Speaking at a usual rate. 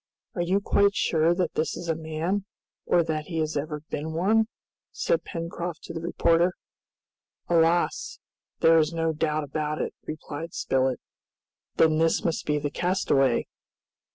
Yes: average, 155 wpm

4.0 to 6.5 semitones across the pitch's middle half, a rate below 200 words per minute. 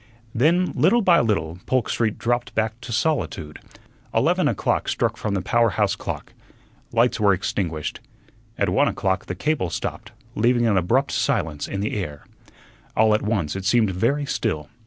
Yes: average, 4.4 semitones; average, 165 wpm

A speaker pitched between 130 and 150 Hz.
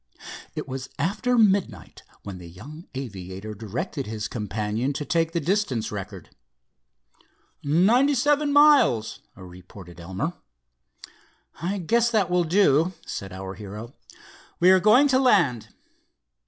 Yes: medium, 140 Hz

